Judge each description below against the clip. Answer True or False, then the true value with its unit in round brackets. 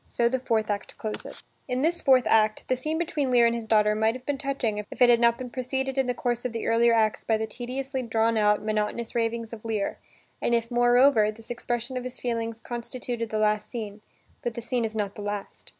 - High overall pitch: True (235 Hz)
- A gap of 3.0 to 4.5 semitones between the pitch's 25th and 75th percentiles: False (2.4 semitones)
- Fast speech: True (230 wpm)